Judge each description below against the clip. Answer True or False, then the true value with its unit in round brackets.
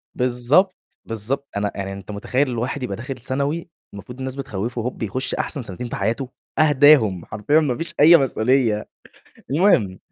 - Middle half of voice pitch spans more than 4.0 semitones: True (4.5 semitones)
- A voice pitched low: True (125 Hz)